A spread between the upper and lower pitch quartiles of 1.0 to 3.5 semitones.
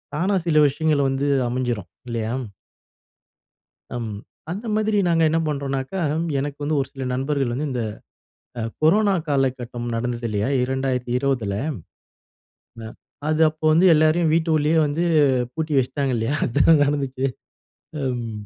No: average, 4.0 semitones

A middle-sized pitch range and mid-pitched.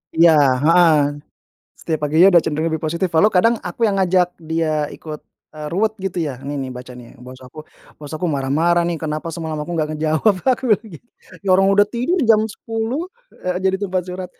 Yes: average, 4.0 semitones; medium, 170 Hz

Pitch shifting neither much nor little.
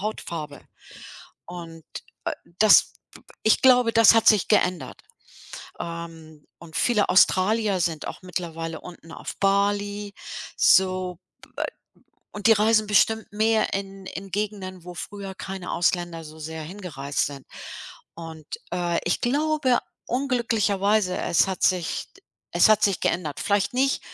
Yes: average, 4.1 semitones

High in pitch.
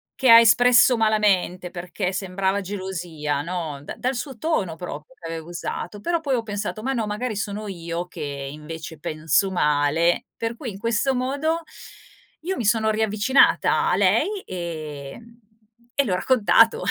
Yes: high, 200 Hz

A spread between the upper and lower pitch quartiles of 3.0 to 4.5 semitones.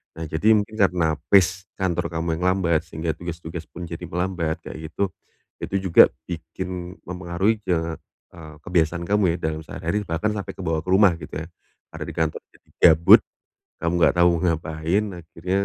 No: narrow, 2.4 semitones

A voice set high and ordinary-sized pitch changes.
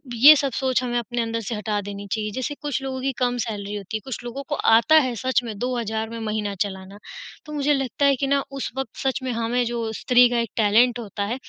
Yes: high, 240 Hz; average, 3.3 semitones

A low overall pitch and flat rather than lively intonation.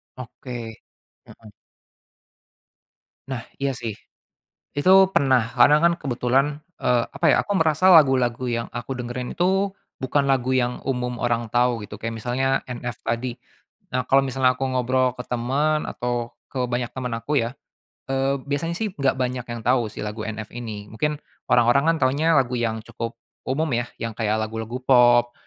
Yes: low, 125 Hz; narrow, 2.3 semitones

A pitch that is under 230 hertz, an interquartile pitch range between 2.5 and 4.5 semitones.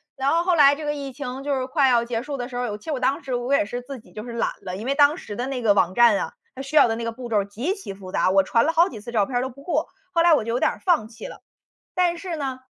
No: very high, 255 Hz; average, 4.0 semitones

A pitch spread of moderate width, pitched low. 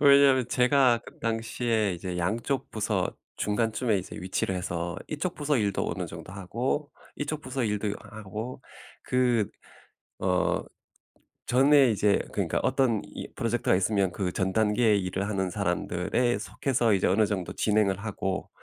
Yes: average, 4.6 semitones; low, 110 Hz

